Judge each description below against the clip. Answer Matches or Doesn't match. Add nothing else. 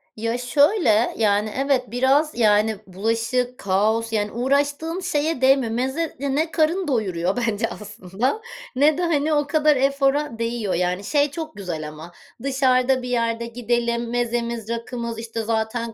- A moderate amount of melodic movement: Matches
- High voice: Matches